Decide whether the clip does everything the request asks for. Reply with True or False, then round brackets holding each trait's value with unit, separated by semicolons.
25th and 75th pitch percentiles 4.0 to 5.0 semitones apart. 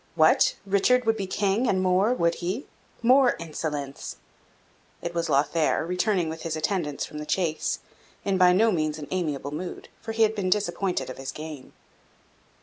True (4.4 semitones)